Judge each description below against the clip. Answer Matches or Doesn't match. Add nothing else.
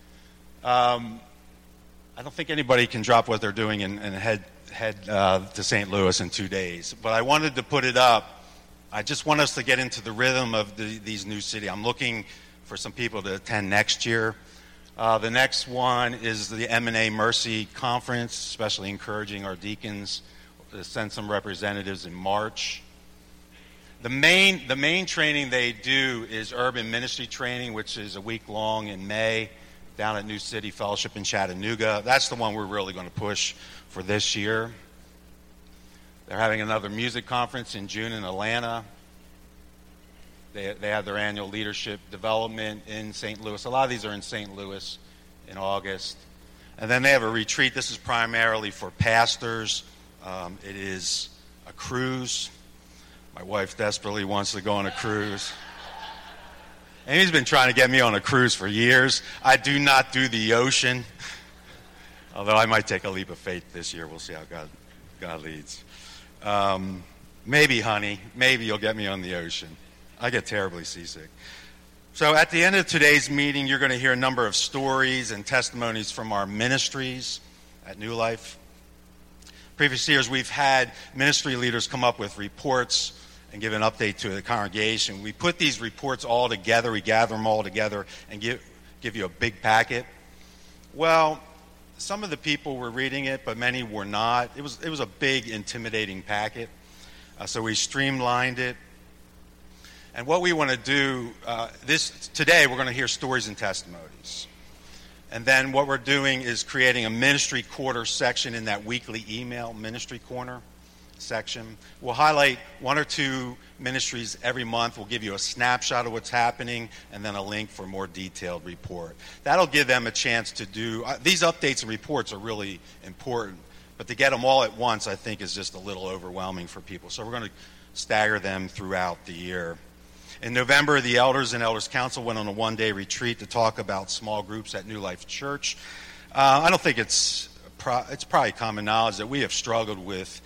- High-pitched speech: Doesn't match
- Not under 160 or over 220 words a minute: Matches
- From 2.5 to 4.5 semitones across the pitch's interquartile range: Doesn't match